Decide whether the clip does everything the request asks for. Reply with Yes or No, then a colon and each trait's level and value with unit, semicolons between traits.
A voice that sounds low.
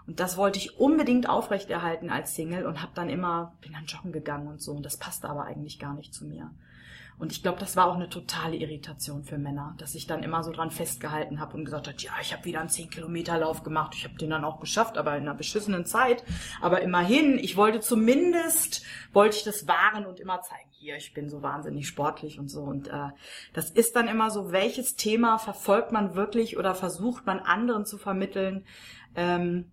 No: medium, 170 Hz